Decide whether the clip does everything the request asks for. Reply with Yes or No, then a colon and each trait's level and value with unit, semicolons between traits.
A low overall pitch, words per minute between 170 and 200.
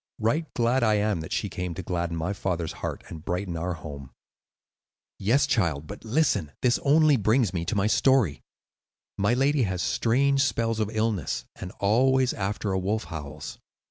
Yes: low, 105 Hz; average, 175 wpm